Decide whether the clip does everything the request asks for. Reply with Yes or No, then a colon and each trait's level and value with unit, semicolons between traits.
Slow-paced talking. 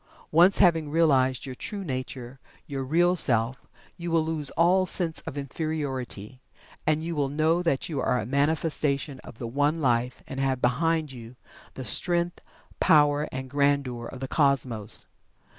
No: average, 155 wpm